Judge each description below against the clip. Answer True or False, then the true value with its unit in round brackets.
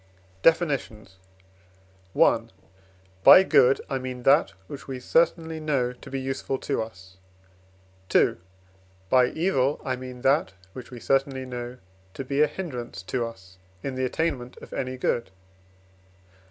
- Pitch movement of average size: False (2.3 semitones)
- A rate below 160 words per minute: True (140 wpm)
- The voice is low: True (130 Hz)